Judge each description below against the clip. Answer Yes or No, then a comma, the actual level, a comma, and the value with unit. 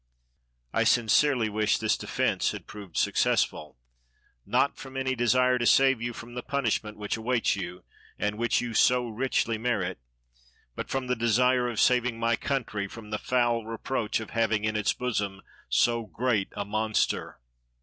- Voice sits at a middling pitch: No, low, 115 Hz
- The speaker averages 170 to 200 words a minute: No, average, 160 wpm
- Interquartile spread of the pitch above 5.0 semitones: No, average, 2.8 semitones